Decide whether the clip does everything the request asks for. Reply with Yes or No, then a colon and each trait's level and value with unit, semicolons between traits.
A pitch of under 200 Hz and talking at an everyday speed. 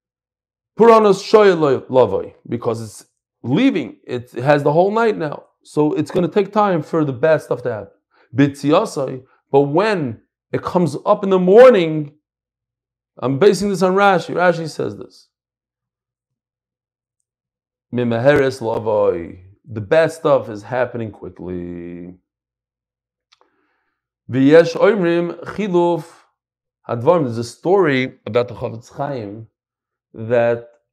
No: low, 135 Hz; slow, 100 wpm